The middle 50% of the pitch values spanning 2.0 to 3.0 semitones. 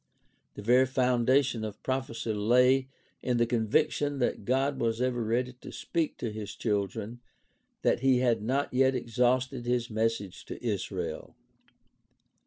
Yes: narrow, 2.5 semitones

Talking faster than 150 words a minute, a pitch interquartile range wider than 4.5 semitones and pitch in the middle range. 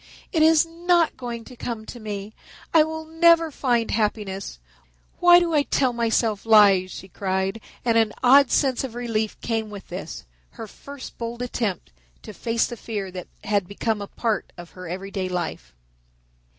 No: average, 170 wpm; average, 5.0 semitones; high, 225 Hz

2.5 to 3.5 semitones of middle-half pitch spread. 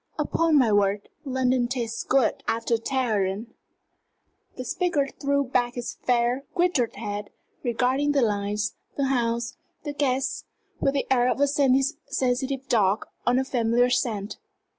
Yes: average, 2.9 semitones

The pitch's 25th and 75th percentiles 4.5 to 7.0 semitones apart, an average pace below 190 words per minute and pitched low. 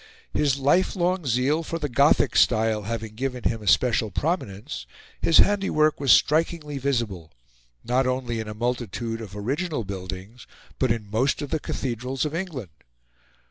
Yes: average, 5.2 semitones; average, 150 wpm; low, 125 Hz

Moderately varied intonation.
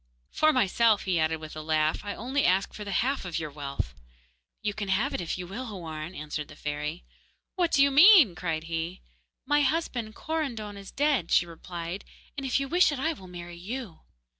No: wide, 8.4 semitones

